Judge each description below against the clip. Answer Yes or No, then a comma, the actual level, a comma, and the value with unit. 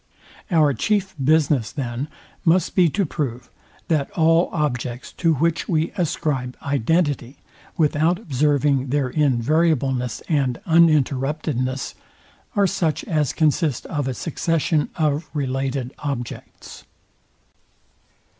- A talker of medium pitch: Yes, medium, 150 Hz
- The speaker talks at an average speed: No, slow, 105 wpm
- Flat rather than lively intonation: No, average, 3.6 semitones